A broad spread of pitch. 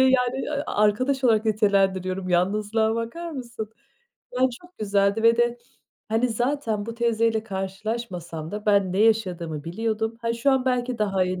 No: average, 3.3 semitones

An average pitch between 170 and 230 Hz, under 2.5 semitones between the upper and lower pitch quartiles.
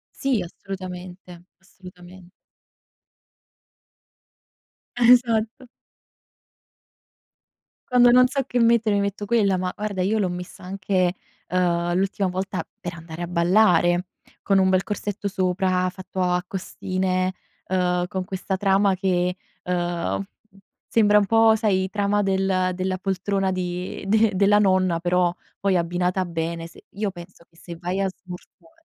Yes: medium, 185 Hz; narrow, 2.1 semitones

